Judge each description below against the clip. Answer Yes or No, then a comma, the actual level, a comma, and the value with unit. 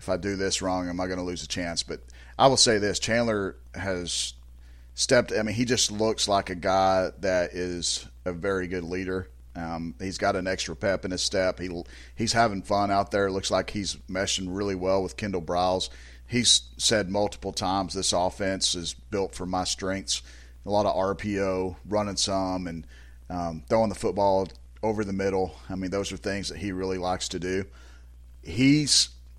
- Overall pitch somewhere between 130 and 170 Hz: No, very low, 95 Hz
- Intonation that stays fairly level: No, average, 3.0 semitones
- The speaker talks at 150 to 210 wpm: Yes, average, 195 wpm